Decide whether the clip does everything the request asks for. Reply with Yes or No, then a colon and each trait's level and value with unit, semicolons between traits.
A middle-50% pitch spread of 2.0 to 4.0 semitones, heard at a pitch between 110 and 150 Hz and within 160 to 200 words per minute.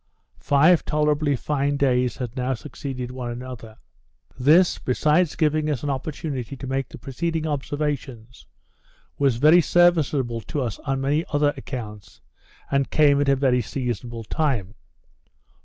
No: average, 3.2 semitones; medium, 140 Hz; average, 140 wpm